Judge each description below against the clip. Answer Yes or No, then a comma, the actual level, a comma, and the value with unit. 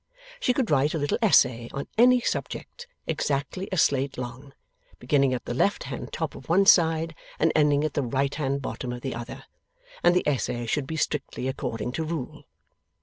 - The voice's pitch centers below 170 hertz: Yes, medium, 140 Hz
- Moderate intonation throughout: Yes, average, 4.1 semitones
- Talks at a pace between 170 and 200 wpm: Yes, average, 190 wpm